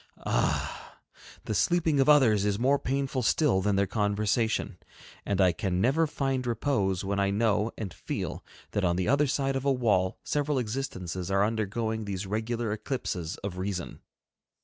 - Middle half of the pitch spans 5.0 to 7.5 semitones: Yes, average, 5.3 semitones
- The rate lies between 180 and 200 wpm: No, average, 165 wpm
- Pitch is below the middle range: Yes, low, 110 Hz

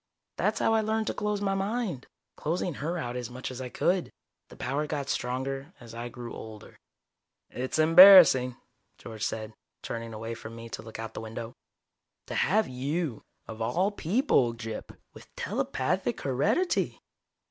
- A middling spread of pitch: No, wide, 7.7 semitones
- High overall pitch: No, low, 130 Hz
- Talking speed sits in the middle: Yes, average, 160 wpm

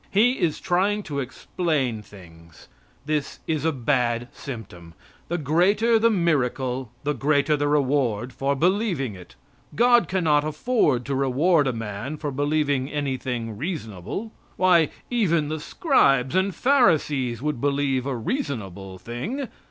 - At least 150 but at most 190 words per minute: No, slow, 135 wpm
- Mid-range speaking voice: Yes, medium, 145 Hz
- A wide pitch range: Yes, wide, 5.8 semitones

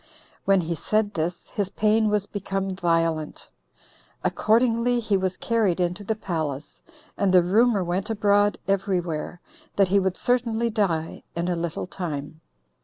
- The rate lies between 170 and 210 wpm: No, average, 150 wpm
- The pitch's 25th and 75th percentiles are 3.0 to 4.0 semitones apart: Yes, average, 3.6 semitones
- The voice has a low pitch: No, high, 195 Hz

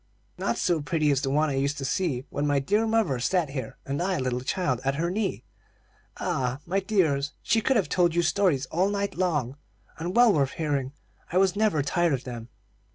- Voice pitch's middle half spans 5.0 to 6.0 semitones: Yes, wide, 5.4 semitones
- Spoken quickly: Yes, fast, 215 wpm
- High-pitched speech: No, medium, 155 Hz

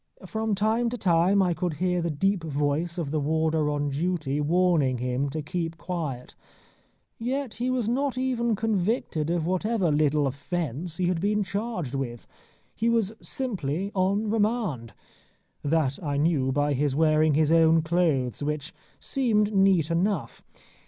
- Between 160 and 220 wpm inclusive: No, average, 150 wpm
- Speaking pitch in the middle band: Yes, medium, 170 Hz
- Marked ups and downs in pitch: Yes, wide, 5.7 semitones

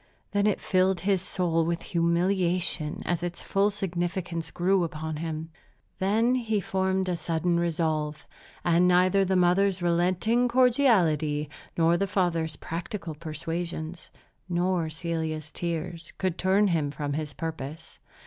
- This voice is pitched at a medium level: Yes, medium, 175 Hz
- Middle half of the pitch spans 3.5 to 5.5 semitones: No, average, 2.7 semitones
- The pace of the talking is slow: Yes, slow, 130 wpm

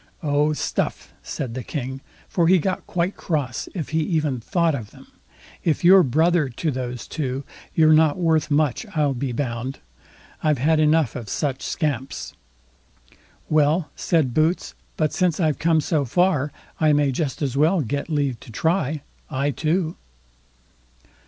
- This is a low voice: No, medium, 150 Hz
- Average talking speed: Yes, average, 155 wpm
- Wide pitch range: No, average, 3.2 semitones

